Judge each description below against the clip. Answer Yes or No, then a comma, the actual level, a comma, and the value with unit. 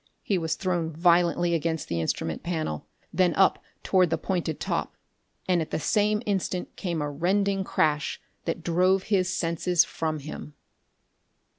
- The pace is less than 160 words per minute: Yes, average, 150 wpm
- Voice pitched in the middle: Yes, medium, 170 Hz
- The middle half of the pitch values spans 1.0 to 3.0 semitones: Yes, narrow, 2.6 semitones